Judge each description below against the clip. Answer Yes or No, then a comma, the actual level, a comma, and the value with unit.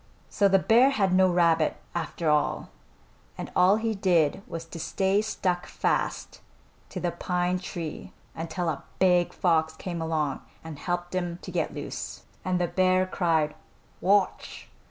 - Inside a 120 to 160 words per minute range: Yes, average, 155 wpm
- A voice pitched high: No, medium, 175 Hz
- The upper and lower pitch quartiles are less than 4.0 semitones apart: Yes, narrow, 2.4 semitones